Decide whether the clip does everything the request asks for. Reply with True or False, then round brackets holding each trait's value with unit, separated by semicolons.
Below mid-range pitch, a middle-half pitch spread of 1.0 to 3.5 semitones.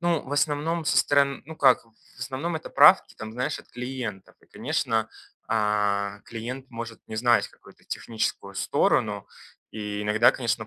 False (120 Hz; 4.2 semitones)